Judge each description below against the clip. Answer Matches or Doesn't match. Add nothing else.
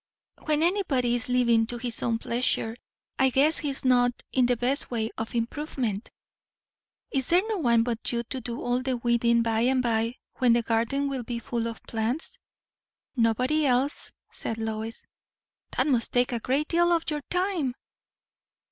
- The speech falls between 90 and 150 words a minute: Doesn't match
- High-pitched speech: Matches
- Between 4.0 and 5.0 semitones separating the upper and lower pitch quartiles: Doesn't match